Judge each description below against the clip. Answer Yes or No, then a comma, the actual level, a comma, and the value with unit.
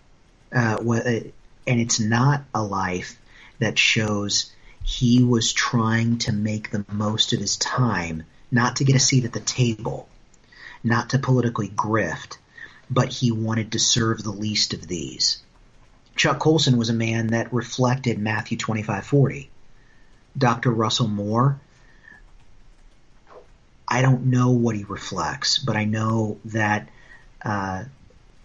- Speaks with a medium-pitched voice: No, low, 115 Hz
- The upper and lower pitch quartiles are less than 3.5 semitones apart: Yes, narrow, 2.6 semitones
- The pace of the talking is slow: Yes, slow, 130 wpm